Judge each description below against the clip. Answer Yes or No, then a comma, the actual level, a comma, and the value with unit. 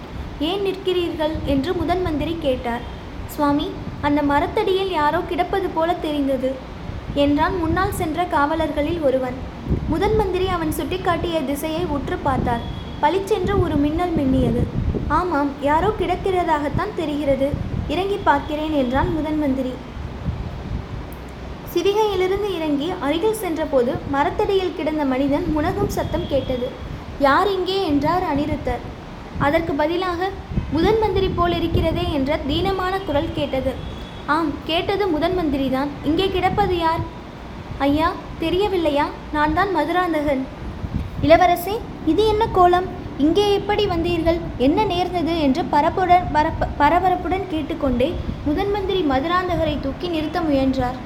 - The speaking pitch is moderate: No, very high, 325 Hz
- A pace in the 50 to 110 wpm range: Yes, average, 105 wpm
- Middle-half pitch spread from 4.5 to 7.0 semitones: No, average, 3.8 semitones